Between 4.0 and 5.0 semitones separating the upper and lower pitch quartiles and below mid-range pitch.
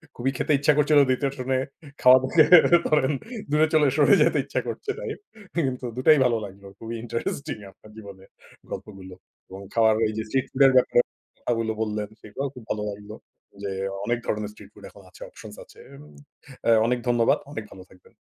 Yes: average, 4.4 semitones; low, 120 Hz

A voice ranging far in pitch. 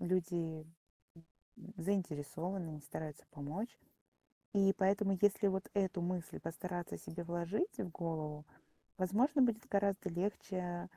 No: average, 3.1 semitones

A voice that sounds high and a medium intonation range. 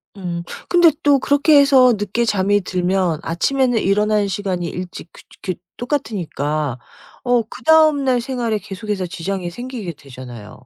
No: high, 205 Hz; wide, 6.2 semitones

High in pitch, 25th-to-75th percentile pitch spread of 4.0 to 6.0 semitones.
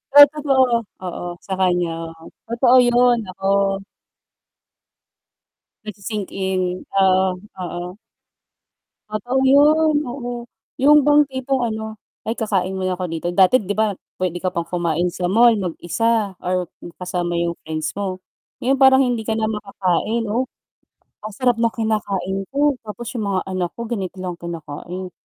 Yes: high, 200 Hz; average, 4.8 semitones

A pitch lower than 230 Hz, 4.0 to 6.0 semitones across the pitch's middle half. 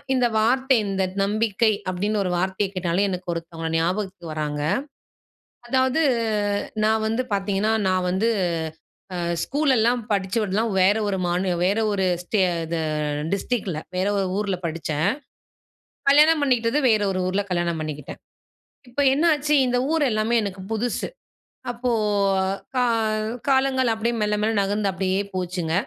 Yes: high, 205 Hz; average, 4.3 semitones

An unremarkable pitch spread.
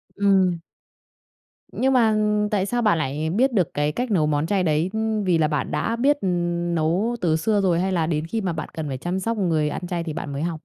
Yes: average, 4.8 semitones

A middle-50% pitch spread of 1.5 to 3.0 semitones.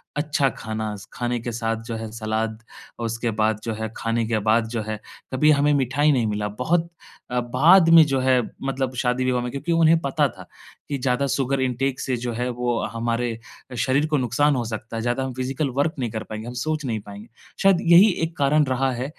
No: average, 3.5 semitones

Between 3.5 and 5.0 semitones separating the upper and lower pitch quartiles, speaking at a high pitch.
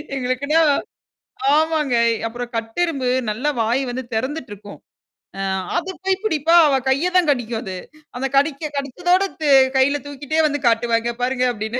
Yes: average, 4.7 semitones; very high, 270 Hz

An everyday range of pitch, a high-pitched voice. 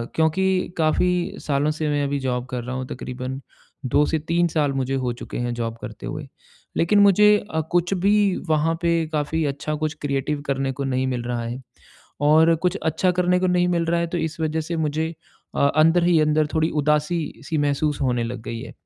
No: average, 3.9 semitones; medium, 155 Hz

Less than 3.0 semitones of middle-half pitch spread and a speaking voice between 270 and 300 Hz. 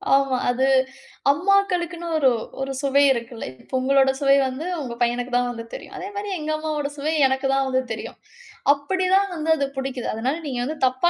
No: average, 3.5 semitones; very high, 275 Hz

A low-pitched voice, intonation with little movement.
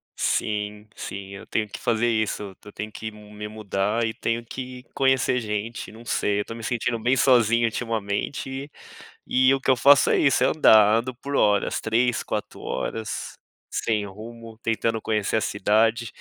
Yes: low, 110 Hz; narrow, 2.3 semitones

